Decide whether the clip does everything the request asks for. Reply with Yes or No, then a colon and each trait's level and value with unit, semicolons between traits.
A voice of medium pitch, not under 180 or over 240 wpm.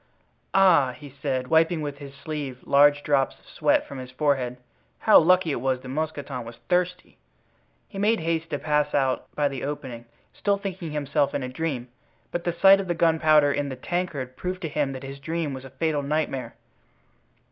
Yes: medium, 145 Hz; average, 190 wpm